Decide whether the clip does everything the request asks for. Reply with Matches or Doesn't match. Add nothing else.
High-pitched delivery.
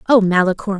Matches